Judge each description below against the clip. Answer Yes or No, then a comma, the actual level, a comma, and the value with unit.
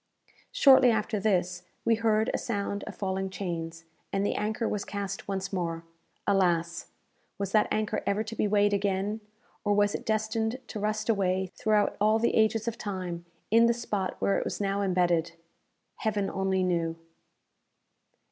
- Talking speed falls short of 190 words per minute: Yes, average, 165 wpm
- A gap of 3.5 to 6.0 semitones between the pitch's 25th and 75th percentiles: No, narrow, 2.4 semitones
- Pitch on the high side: Yes, high, 200 Hz